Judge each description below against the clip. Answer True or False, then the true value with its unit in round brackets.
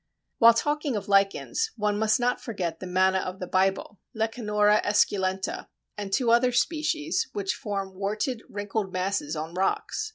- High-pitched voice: True (205 Hz)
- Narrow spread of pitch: False (3.5 semitones)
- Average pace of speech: True (155 wpm)